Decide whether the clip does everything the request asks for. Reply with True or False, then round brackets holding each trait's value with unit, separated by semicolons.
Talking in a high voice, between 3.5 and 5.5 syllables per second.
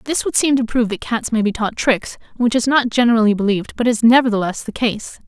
False (230 Hz; 6.1 syllables/s)